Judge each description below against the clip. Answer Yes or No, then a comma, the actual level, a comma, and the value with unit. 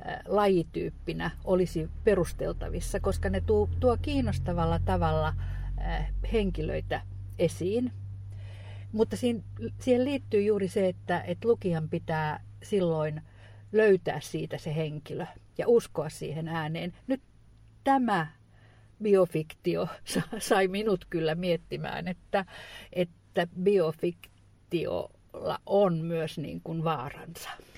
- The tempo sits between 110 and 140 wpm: No, slow, 95 wpm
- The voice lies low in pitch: No, medium, 160 Hz